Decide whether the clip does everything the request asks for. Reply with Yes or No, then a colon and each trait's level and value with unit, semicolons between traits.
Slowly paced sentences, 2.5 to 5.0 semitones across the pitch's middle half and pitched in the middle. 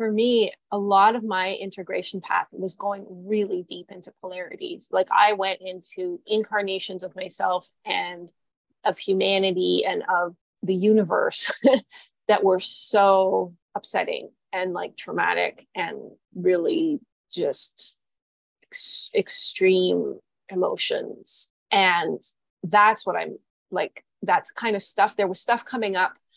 No: slow, 125 wpm; average, 3.7 semitones; high, 195 Hz